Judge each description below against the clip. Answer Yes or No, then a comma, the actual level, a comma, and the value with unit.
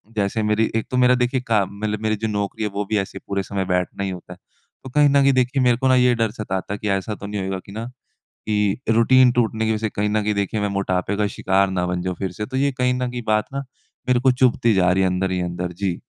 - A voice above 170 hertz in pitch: No, low, 105 Hz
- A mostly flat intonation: No, average, 4.0 semitones